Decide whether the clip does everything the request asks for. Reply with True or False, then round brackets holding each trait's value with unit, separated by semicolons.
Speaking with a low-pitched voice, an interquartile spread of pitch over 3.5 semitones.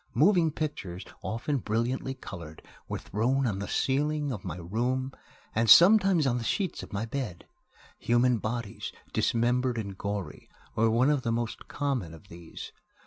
True (120 Hz; 4.7 semitones)